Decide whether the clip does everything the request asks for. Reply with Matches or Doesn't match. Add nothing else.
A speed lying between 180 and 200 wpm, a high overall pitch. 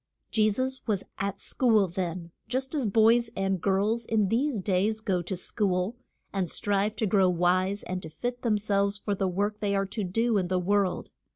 Matches